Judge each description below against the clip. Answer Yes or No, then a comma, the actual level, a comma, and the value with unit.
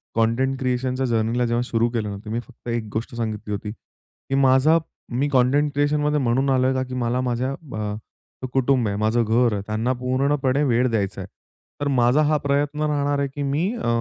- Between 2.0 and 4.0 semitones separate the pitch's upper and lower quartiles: Yes, average, 3.2 semitones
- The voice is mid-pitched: No, low, 125 Hz